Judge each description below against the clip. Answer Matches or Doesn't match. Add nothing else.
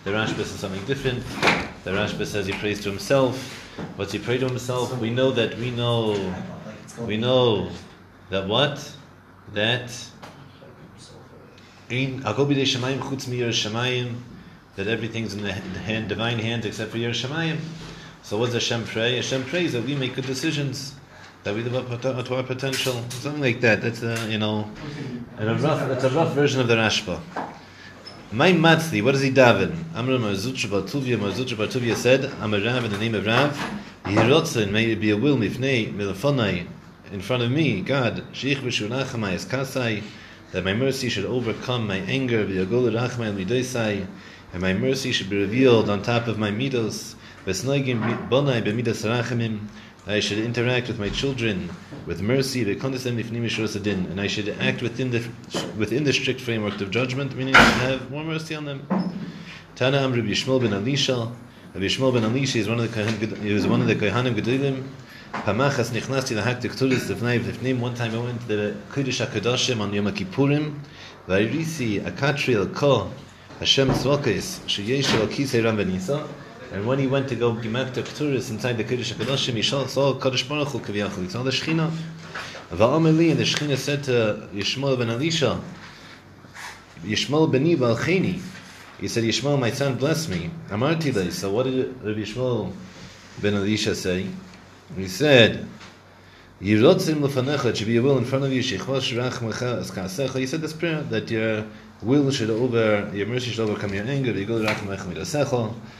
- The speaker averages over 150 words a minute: Matches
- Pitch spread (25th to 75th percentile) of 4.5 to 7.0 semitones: Doesn't match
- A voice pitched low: Matches